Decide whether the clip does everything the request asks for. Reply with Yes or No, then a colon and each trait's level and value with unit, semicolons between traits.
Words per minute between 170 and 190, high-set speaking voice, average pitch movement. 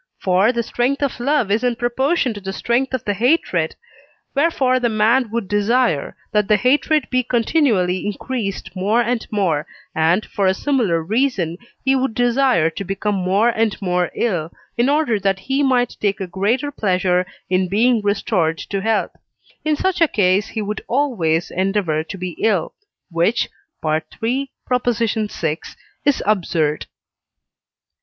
No: average, 155 wpm; high, 215 Hz; average, 5.0 semitones